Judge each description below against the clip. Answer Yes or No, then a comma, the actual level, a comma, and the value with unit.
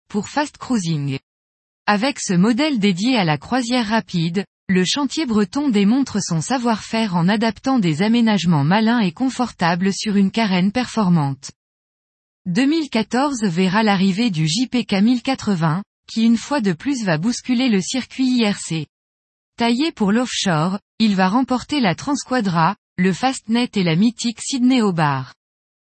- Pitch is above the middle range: Yes, high, 215 Hz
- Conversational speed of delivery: No, slow, 135 wpm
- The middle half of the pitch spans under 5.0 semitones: No, wide, 5.5 semitones